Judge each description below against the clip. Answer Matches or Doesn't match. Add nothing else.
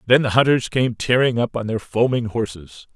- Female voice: Doesn't match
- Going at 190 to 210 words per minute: Matches